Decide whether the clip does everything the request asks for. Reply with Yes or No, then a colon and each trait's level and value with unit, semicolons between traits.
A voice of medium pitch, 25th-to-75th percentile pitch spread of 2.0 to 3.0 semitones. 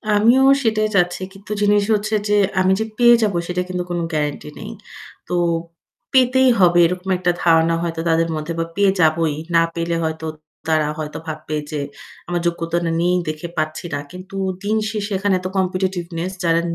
No: medium, 180 Hz; average, 3.7 semitones